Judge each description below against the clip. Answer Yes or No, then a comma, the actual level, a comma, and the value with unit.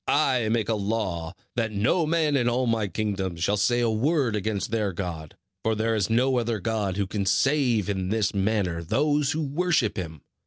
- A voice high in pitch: No, low, 110 Hz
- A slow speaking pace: No, average, 195 wpm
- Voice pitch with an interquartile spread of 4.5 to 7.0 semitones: No, average, 4.0 semitones